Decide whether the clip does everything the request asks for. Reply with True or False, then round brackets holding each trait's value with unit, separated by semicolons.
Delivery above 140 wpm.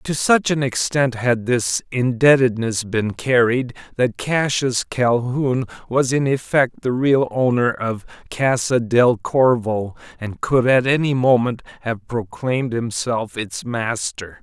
False (135 wpm)